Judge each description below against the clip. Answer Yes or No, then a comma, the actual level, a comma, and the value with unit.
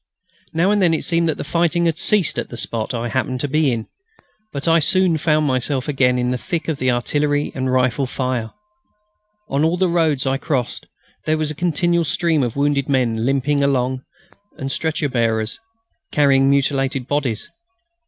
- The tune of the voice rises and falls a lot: No, average, 3.8 semitones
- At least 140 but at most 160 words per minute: No, average, 185 wpm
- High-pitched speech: No, medium, 140 Hz